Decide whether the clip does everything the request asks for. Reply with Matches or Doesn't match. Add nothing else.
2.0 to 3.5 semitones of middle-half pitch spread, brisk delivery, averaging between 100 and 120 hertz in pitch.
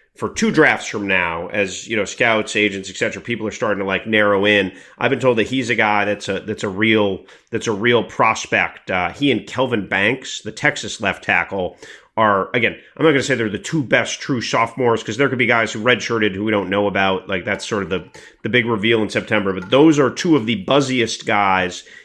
Matches